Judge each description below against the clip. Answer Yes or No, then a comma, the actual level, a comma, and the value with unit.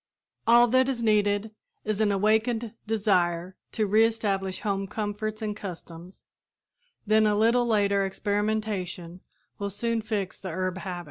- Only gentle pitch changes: Yes, narrow, 2.2 semitones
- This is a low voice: No, high, 210 Hz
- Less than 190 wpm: Yes, average, 140 wpm